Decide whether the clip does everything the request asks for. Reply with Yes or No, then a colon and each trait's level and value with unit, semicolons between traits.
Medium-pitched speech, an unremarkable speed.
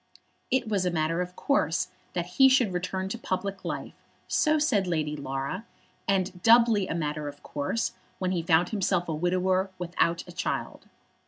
Yes: medium, 180 Hz; average, 170 wpm